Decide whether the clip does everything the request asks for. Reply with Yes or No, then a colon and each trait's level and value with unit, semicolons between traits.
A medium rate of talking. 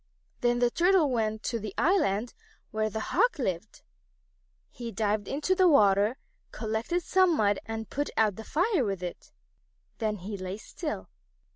Yes: average, 155 wpm